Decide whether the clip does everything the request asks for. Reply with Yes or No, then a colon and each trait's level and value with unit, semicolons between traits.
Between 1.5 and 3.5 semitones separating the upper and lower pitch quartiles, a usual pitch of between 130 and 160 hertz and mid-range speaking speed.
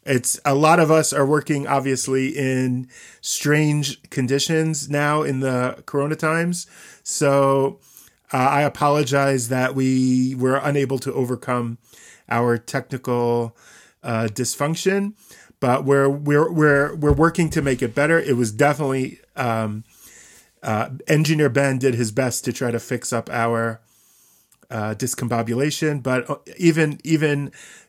No: average, 2.8 semitones; low, 135 Hz; slow, 130 wpm